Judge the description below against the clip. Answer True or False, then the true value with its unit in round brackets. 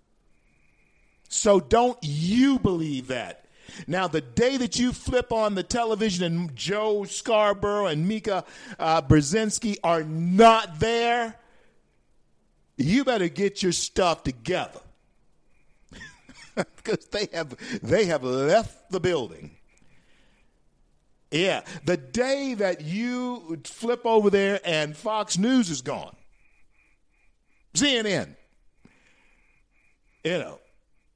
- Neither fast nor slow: False (105 wpm)